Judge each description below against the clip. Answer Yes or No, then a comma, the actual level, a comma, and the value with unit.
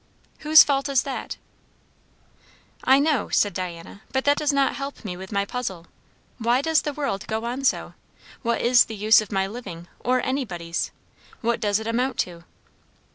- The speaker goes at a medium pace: Yes, average, 175 wpm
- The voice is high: Yes, high, 235 Hz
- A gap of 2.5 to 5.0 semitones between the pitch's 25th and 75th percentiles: No, wide, 5.5 semitones